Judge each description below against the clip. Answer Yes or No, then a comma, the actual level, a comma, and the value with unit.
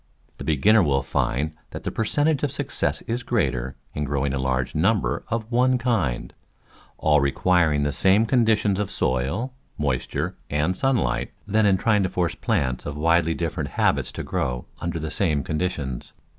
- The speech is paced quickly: No, average, 170 wpm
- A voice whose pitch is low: Yes, very low, 85 Hz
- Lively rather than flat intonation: Yes, wide, 7.5 semitones